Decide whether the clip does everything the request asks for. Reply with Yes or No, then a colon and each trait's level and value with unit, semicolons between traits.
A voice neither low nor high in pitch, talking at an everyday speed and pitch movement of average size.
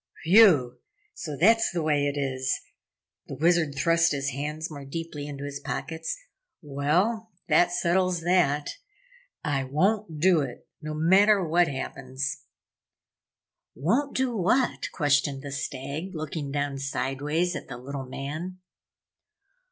No: medium, 150 Hz; slow, 130 wpm; average, 4.0 semitones